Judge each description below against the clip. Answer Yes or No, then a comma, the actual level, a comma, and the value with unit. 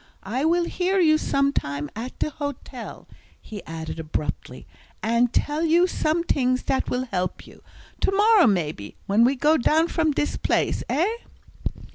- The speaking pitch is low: No, very high, 280 Hz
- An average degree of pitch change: No, wide, 7.0 semitones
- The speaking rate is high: No, average, 155 wpm